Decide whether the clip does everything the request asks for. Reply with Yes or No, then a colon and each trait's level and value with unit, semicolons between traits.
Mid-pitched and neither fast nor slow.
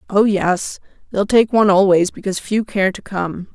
No: high, 195 Hz; average, 185 wpm